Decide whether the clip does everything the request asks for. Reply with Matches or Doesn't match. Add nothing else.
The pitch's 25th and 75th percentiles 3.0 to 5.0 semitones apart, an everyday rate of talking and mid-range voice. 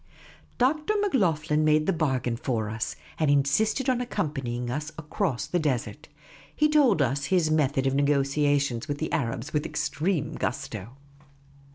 Matches